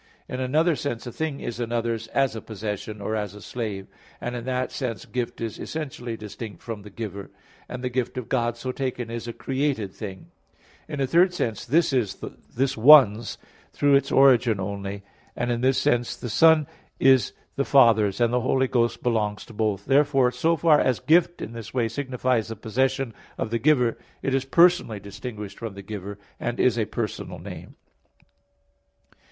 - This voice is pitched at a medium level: No, low, 120 Hz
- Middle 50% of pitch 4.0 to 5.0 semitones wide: No, average, 3.4 semitones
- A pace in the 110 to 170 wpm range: No, average, 185 wpm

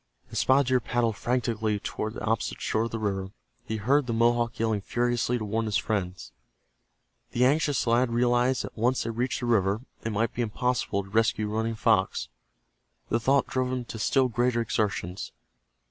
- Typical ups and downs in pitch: No, narrow, 2.3 semitones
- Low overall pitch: Yes, low, 115 Hz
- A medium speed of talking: Yes, average, 180 wpm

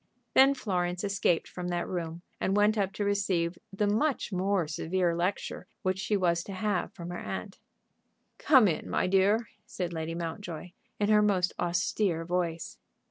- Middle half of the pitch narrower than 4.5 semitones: Yes, average, 2.9 semitones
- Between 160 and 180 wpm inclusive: Yes, average, 165 wpm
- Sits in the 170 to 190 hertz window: Yes, medium, 185 Hz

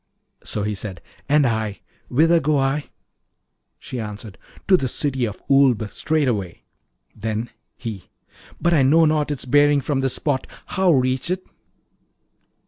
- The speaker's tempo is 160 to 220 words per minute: No, average, 140 wpm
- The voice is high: No, low, 135 Hz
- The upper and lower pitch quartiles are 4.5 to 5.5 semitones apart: Yes, average, 5.2 semitones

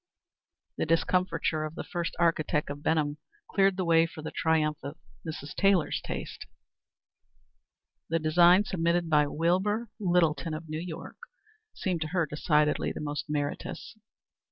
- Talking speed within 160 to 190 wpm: No, average, 140 wpm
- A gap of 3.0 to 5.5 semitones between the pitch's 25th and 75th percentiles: No, narrow, 2.5 semitones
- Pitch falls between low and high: Yes, medium, 165 Hz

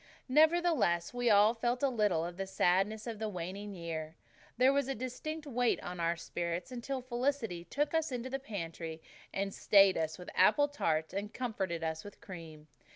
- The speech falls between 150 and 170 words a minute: No, average, 180 wpm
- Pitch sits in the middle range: No, high, 205 Hz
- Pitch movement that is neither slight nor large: No, wide, 6.8 semitones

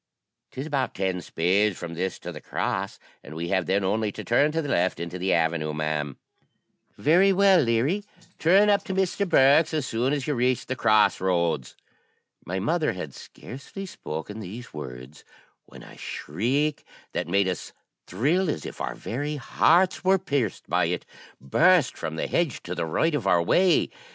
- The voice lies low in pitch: Yes, low, 115 Hz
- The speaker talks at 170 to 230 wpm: Yes, average, 180 wpm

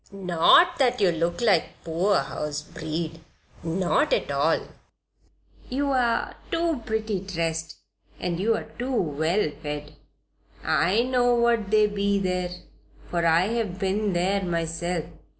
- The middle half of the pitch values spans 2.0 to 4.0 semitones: No, average, 5.2 semitones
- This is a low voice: No, high, 190 Hz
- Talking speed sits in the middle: No, slow, 120 wpm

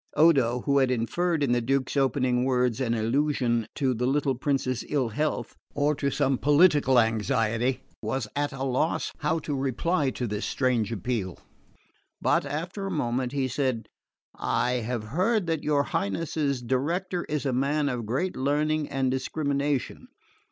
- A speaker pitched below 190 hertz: Yes, low, 135 Hz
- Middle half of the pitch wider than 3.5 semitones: No, average, 3.2 semitones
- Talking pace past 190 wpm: No, average, 160 wpm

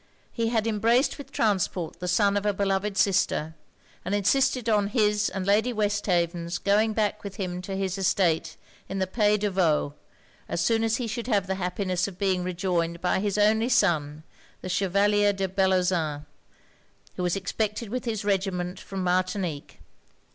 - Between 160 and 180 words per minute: Yes, average, 170 wpm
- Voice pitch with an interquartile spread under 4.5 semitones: Yes, narrow, 2.6 semitones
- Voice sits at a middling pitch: No, high, 195 Hz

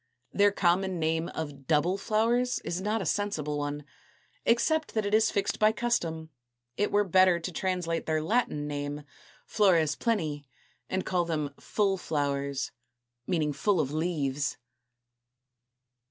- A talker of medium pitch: Yes, medium, 170 Hz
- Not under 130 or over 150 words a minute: Yes, average, 140 wpm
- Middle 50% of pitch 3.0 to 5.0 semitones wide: No, wide, 5.4 semitones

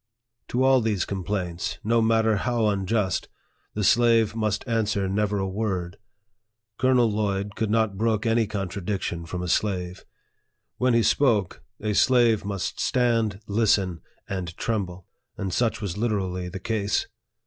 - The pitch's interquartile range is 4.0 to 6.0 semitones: No, average, 2.9 semitones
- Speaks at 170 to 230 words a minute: No, average, 140 wpm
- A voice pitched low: Yes, low, 105 Hz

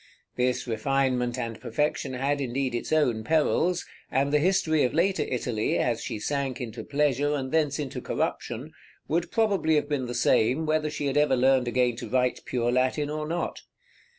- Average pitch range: Yes, average, 3.5 semitones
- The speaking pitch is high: No, low, 135 Hz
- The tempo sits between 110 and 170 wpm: No, average, 180 wpm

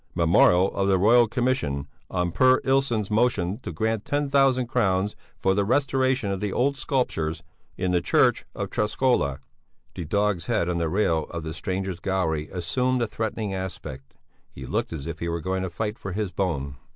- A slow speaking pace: No, average, 185 wpm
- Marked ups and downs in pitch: Yes, wide, 6.0 semitones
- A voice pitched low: Yes, very low, 95 Hz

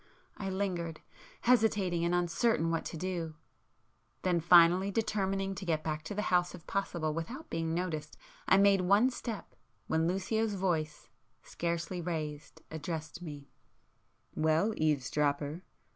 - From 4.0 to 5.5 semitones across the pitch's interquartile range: No, average, 3.4 semitones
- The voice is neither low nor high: Yes, medium, 175 Hz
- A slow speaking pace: Yes, slow, 130 wpm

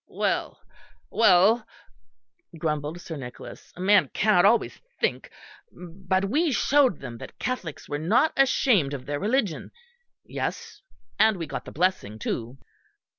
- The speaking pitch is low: No, medium, 185 Hz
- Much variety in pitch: Yes, wide, 7.1 semitones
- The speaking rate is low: Yes, slow, 130 wpm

